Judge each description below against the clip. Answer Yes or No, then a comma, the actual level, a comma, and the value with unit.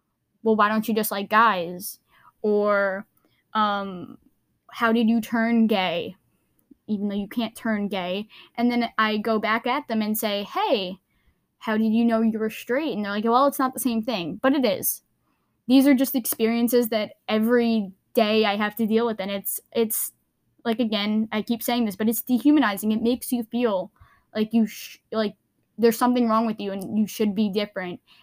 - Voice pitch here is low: No, high, 220 Hz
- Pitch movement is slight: Yes, narrow, 2.2 semitones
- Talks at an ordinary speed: Yes, average, 195 wpm